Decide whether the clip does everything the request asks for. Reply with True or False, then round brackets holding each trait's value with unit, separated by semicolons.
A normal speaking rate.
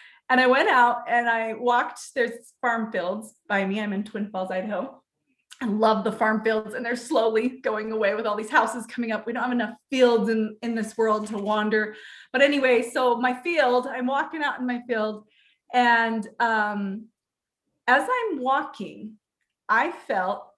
True (180 wpm)